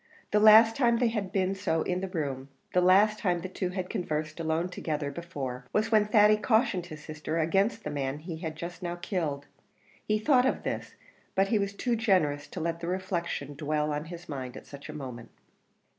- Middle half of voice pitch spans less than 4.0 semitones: No, average, 5.1 semitones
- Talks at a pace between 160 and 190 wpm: No, fast, 205 wpm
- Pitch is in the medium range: Yes, medium, 175 Hz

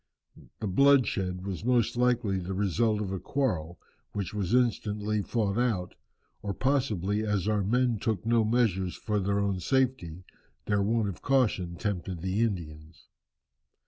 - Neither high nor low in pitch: No, low, 105 Hz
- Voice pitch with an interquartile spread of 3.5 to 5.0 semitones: Yes, average, 3.8 semitones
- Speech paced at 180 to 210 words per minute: No, average, 145 wpm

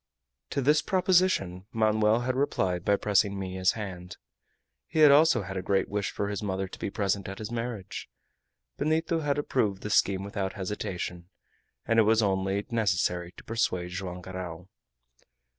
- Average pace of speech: Yes, average, 160 wpm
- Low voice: Yes, low, 100 Hz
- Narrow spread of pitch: No, average, 3.6 semitones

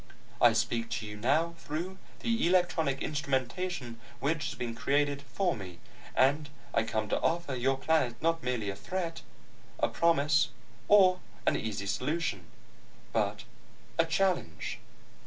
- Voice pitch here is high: No, medium, 145 Hz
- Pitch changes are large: Yes, wide, 6.1 semitones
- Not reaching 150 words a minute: Yes, average, 140 wpm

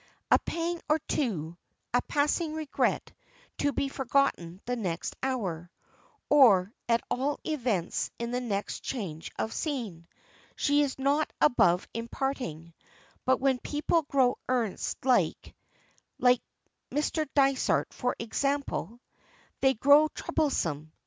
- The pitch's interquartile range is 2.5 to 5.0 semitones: No, wide, 5.6 semitones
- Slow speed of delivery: Yes, slow, 120 wpm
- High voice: Yes, very high, 255 Hz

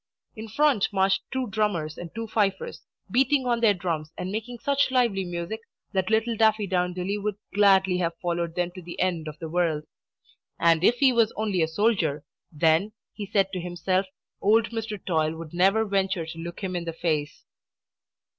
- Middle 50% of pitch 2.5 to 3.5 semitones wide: No, average, 4.2 semitones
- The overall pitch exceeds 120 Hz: Yes, high, 190 Hz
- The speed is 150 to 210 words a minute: Yes, average, 180 wpm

